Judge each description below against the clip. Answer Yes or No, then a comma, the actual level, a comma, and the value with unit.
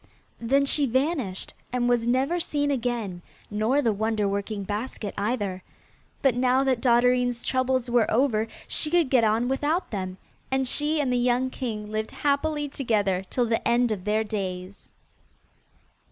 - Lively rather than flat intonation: No, average, 3.8 semitones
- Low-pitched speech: No, high, 245 Hz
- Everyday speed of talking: Yes, average, 155 wpm